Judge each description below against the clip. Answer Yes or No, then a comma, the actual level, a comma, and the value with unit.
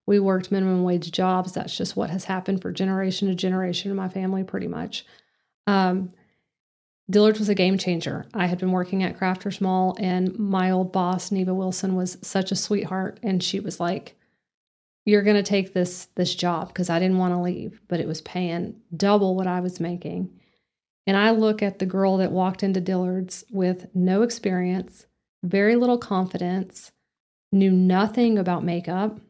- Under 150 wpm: No, average, 180 wpm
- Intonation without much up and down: Yes, narrow, 1.5 semitones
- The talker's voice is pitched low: No, medium, 185 Hz